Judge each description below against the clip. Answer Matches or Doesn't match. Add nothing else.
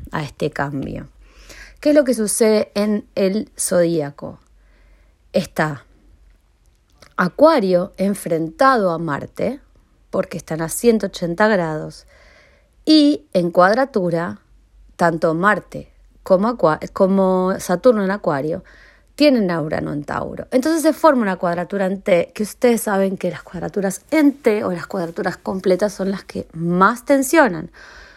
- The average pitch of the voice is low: Doesn't match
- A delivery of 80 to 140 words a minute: Matches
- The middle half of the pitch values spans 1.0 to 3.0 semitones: Doesn't match